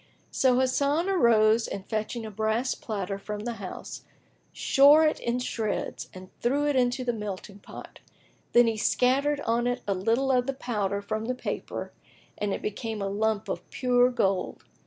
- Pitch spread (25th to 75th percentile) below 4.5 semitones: Yes, average, 3.3 semitones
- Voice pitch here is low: No, high, 230 Hz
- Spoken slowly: No, average, 175 wpm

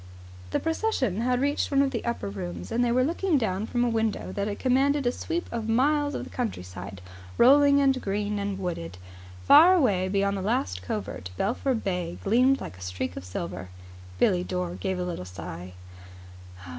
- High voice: Yes, high, 205 Hz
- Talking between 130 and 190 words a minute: Yes, average, 180 wpm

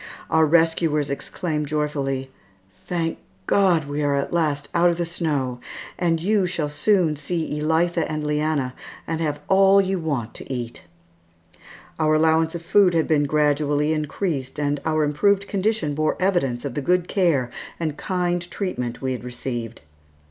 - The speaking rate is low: No, average, 155 wpm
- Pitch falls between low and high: Yes, medium, 155 Hz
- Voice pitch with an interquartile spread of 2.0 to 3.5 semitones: Yes, average, 3.1 semitones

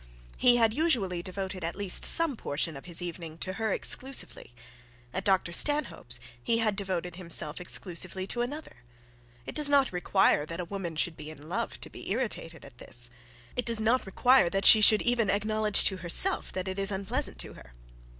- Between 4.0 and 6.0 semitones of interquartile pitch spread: Yes, average, 5.1 semitones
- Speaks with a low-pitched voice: No, high, 195 Hz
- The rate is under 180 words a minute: No, average, 190 wpm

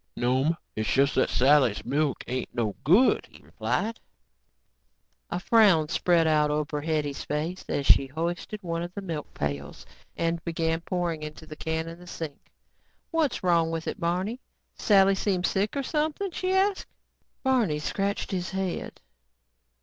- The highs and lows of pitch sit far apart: No, average, 4.4 semitones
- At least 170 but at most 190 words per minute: No, average, 150 wpm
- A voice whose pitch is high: No, medium, 165 Hz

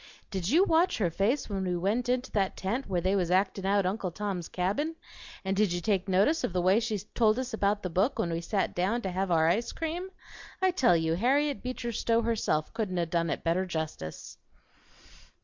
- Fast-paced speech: Yes, fast, 215 wpm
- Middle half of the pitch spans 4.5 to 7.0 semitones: Yes, average, 4.8 semitones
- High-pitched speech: Yes, high, 195 Hz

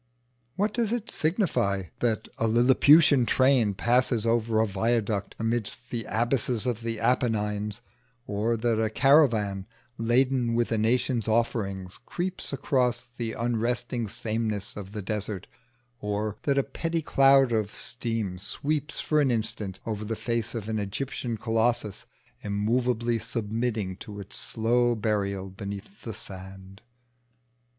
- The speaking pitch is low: Yes, low, 115 Hz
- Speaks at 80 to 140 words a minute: Yes, slow, 135 wpm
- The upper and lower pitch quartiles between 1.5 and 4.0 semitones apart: Yes, average, 2.9 semitones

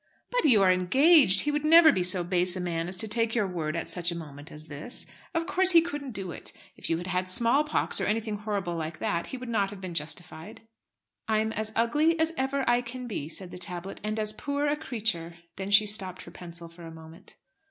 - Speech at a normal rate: No, fast, 235 wpm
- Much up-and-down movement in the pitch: Yes, wide, 6.3 semitones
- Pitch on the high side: Yes, high, 200 Hz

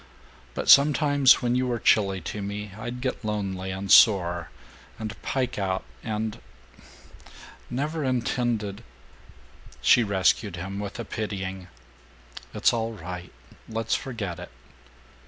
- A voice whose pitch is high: No, low, 105 Hz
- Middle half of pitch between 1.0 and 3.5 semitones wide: No, average, 4.0 semitones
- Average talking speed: No, slow, 125 wpm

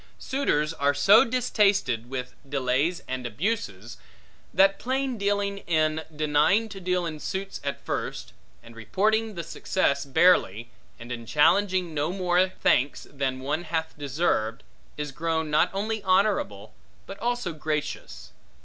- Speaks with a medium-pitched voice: Yes, medium, 160 Hz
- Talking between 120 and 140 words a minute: Yes, slow, 135 wpm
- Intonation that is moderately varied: No, wide, 6.1 semitones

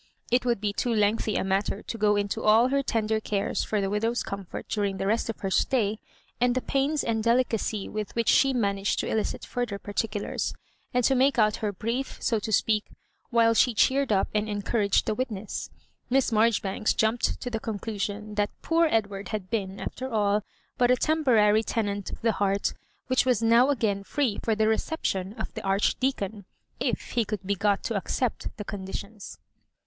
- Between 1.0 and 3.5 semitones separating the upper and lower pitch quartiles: Yes, average, 2.8 semitones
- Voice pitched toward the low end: No, high, 215 Hz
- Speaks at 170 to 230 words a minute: Yes, average, 195 wpm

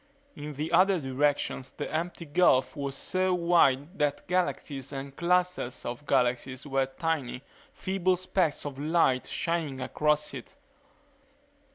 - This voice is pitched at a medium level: Yes, medium, 150 Hz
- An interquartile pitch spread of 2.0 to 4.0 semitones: No, average, 4.4 semitones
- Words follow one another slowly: Yes, slow, 130 wpm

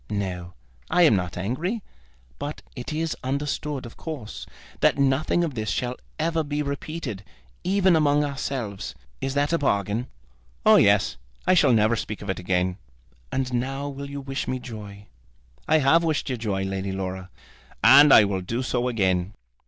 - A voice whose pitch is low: Yes, low, 130 Hz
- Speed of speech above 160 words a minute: Yes, average, 170 wpm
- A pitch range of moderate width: No, wide, 6.3 semitones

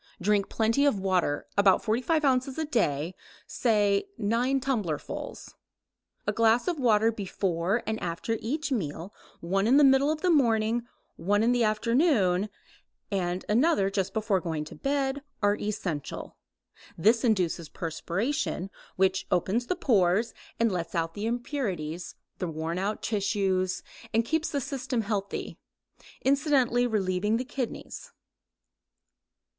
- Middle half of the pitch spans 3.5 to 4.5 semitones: No, average, 5.2 semitones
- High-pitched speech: Yes, high, 215 Hz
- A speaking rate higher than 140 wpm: No, slow, 135 wpm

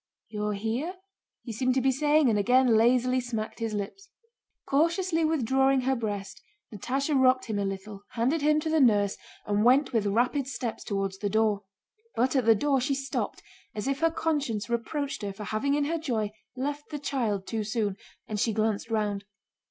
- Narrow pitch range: No, average, 4.7 semitones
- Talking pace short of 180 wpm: No, average, 185 wpm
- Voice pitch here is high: Yes, high, 245 Hz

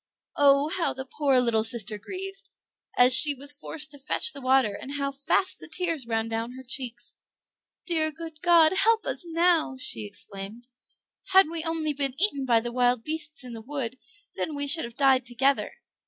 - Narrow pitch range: No, average, 4.5 semitones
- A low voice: No, very high, 275 Hz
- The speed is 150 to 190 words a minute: Yes, average, 185 wpm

